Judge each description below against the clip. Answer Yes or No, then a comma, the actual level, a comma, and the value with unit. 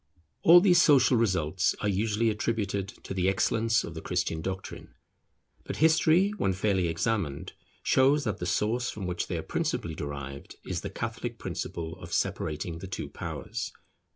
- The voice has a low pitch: Yes, low, 100 Hz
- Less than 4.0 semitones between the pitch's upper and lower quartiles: No, average, 5.2 semitones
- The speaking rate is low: No, average, 160 wpm